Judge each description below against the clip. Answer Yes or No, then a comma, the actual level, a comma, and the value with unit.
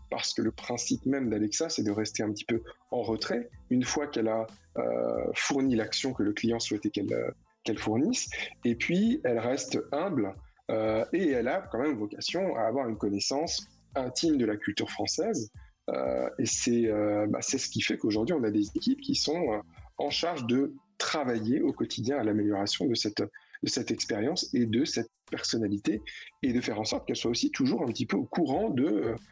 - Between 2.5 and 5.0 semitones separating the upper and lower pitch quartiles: No, wide, 5.5 semitones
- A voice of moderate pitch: No, low, 115 Hz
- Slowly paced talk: No, average, 200 wpm